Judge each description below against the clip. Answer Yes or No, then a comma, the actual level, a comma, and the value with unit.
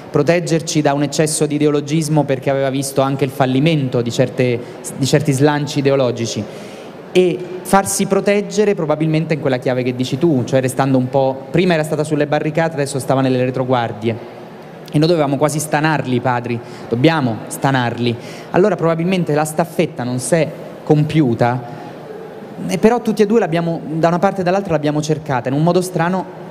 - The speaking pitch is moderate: Yes, medium, 150 Hz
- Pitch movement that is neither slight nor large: Yes, average, 4.4 semitones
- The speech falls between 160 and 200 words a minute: Yes, average, 165 wpm